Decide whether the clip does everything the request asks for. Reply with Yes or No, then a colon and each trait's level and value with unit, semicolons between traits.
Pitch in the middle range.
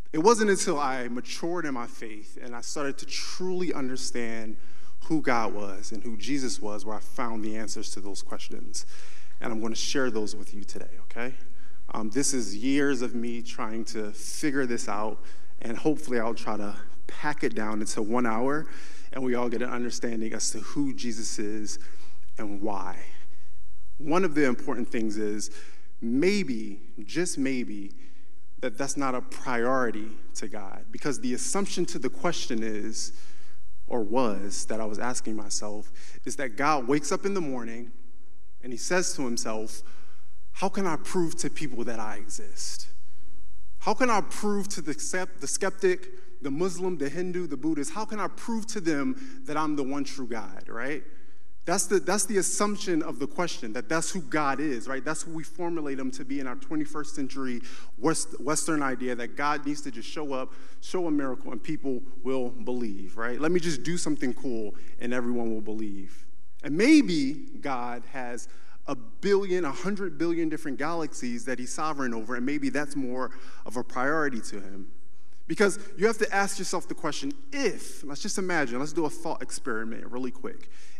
No: low, 125 Hz